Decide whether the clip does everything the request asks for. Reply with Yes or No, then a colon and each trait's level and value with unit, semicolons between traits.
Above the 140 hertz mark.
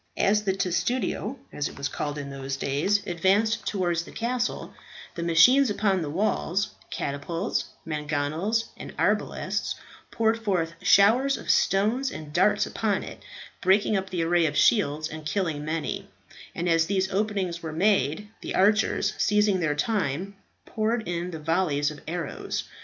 Yes: medium, 185 Hz